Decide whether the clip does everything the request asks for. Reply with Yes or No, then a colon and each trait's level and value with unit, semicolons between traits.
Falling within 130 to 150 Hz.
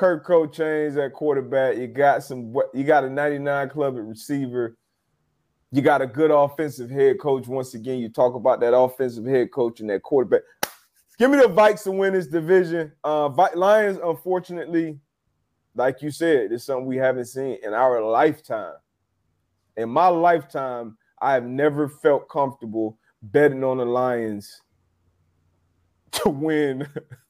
Yes: low, 135 Hz